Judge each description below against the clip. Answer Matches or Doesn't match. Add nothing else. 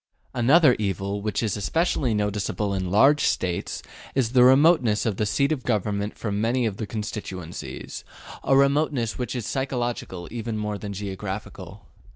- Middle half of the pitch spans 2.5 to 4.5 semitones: Matches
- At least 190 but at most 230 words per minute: Doesn't match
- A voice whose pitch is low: Matches